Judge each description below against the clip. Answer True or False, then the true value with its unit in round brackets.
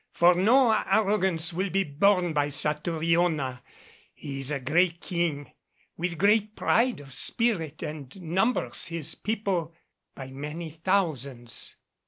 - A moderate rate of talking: False (125 wpm)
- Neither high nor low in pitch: True (170 Hz)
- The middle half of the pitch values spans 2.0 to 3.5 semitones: False (4.7 semitones)